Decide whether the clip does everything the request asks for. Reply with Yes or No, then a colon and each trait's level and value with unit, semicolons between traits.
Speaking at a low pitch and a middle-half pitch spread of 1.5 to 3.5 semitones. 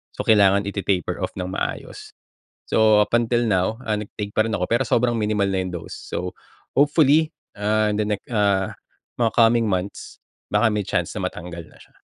Yes: low, 105 Hz; average, 2.9 semitones